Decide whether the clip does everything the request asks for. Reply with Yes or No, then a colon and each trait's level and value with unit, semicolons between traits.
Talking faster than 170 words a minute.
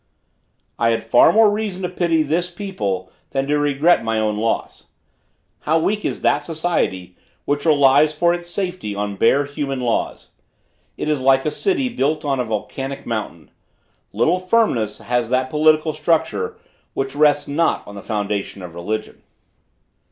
No: average, 160 wpm